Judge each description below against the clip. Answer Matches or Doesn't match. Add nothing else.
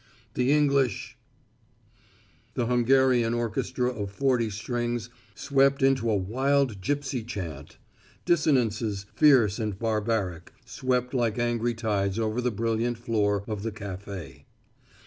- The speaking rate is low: Matches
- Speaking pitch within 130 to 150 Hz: Doesn't match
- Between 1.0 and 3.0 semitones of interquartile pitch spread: Doesn't match